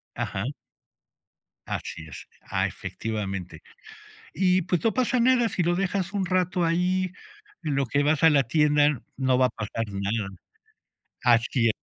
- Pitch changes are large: Yes, wide, 8.2 semitones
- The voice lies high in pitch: No, medium, 150 Hz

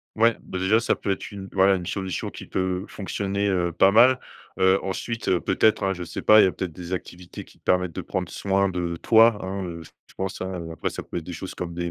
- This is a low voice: Yes, very low, 95 Hz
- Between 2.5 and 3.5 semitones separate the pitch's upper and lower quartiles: No, narrow, 1.8 semitones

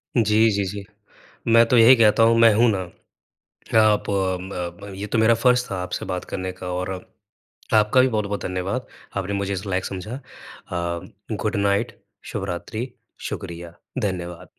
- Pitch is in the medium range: No, low, 100 Hz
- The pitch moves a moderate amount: Yes, average, 3.5 semitones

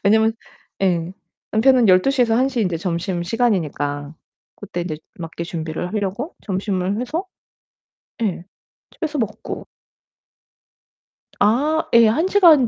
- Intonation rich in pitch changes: Yes, wide, 5.9 semitones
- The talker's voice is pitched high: Yes, high, 205 Hz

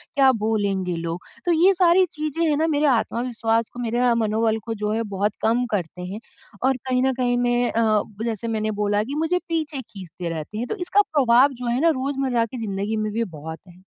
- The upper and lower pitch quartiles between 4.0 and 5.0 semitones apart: Yes, average, 4.4 semitones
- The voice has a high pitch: Yes, high, 230 Hz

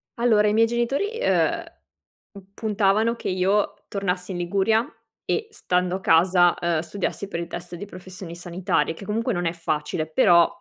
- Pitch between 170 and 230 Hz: Yes, medium, 185 Hz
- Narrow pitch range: No, average, 3.4 semitones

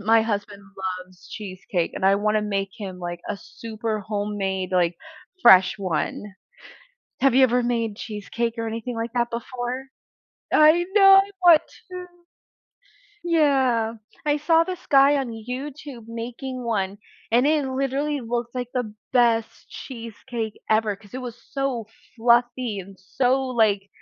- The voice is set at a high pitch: Yes, high, 230 Hz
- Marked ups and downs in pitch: No, average, 4.2 semitones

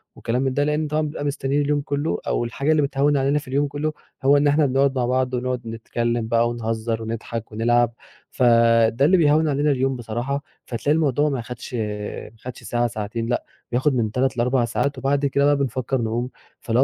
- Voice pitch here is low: Yes, low, 130 Hz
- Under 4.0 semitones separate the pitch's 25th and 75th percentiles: Yes, average, 3.4 semitones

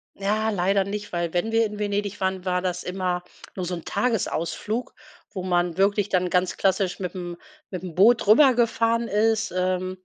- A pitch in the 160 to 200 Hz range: Yes, high, 190 Hz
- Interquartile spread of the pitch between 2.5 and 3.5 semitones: Yes, average, 2.8 semitones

